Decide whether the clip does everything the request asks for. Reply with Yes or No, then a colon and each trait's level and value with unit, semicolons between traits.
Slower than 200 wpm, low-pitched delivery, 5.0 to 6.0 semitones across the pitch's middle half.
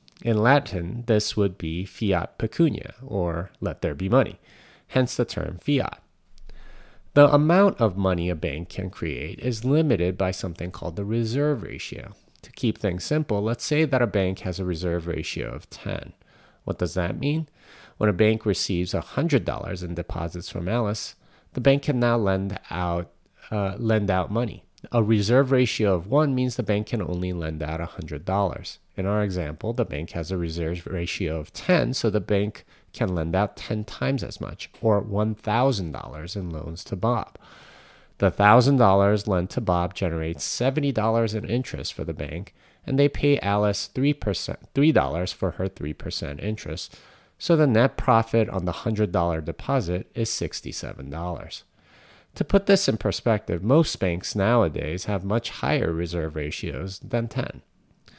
Yes: average, 160 wpm; low, 100 Hz; average, 5.3 semitones